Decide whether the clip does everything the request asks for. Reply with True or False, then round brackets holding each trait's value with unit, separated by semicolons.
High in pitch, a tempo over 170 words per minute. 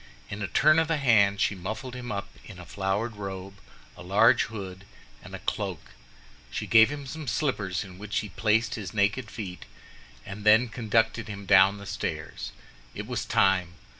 False (105 Hz; 180 wpm)